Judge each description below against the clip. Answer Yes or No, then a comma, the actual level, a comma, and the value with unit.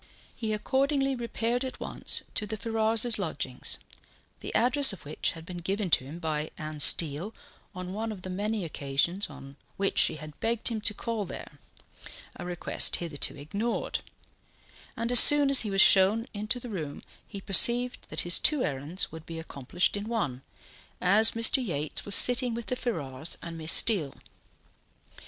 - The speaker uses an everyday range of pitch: No, wide, 6.1 semitones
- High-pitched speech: Yes, high, 200 Hz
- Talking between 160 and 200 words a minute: Yes, average, 170 wpm